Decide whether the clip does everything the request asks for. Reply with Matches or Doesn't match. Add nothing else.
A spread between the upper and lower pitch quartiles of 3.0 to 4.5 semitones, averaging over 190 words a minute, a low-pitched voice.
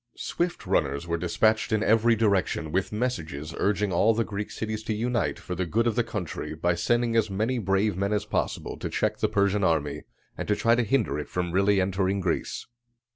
Matches